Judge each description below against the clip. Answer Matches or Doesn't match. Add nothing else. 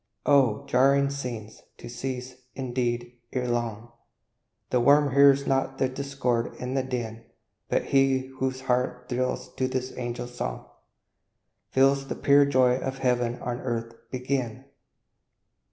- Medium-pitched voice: Doesn't match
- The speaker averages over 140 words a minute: Doesn't match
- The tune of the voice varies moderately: Doesn't match